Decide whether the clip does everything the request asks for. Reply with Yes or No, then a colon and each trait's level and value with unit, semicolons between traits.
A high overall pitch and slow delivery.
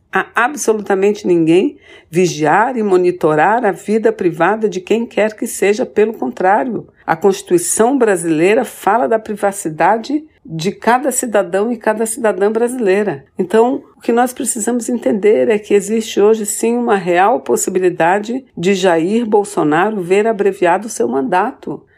No: high, 215 Hz; average, 140 wpm